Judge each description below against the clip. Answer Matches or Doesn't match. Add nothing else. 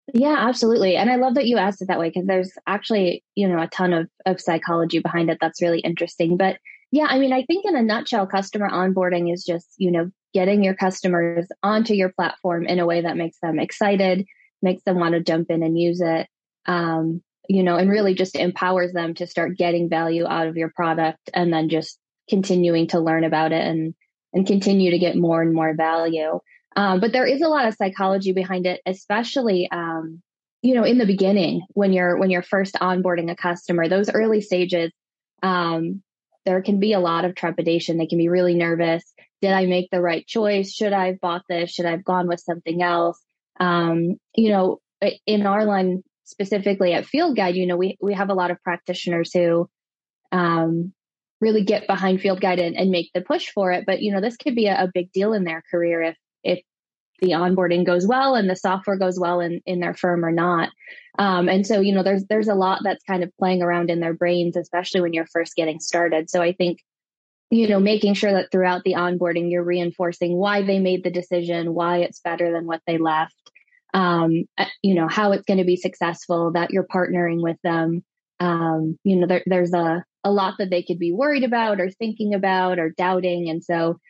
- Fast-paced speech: Matches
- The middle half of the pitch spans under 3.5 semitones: Matches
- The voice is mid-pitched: Matches